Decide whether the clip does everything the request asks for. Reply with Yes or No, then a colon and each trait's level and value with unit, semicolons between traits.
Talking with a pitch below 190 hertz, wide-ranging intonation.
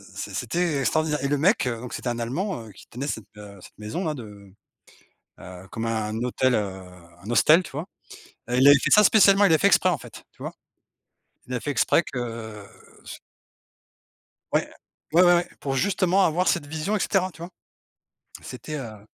Yes: low, 135 Hz; wide, 7.4 semitones